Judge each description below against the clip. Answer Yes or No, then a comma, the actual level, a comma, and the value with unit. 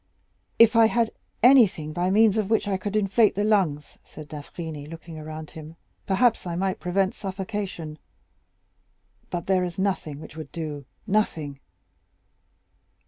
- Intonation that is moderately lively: Yes, average, 4.8 semitones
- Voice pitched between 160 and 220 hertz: Yes, medium, 185 Hz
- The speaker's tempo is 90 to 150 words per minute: Yes, average, 140 wpm